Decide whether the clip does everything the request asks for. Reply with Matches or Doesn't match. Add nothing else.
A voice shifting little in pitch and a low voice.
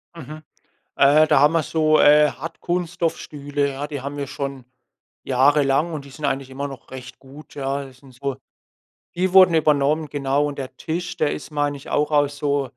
Doesn't match